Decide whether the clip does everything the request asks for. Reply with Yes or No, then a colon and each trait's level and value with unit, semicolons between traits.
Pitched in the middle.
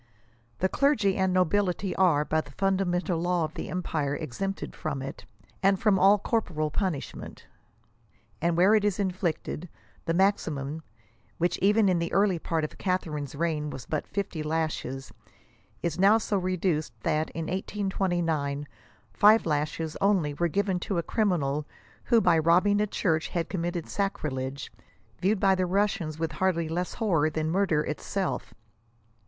Yes: medium, 175 Hz